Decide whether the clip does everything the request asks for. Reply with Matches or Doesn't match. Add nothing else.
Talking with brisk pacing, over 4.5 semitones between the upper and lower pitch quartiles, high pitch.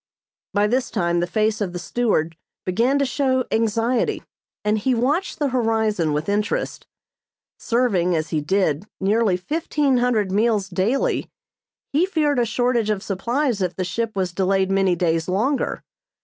Doesn't match